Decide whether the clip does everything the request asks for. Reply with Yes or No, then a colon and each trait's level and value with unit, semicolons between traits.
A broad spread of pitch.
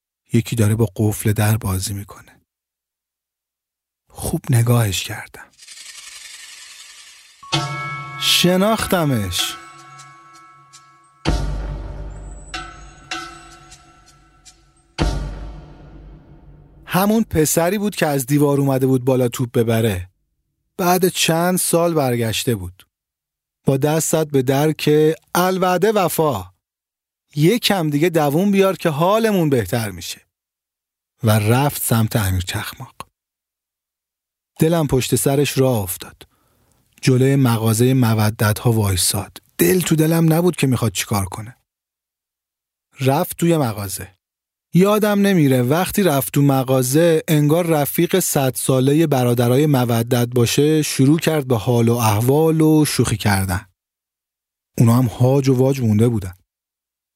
Yes: wide, 6.9 semitones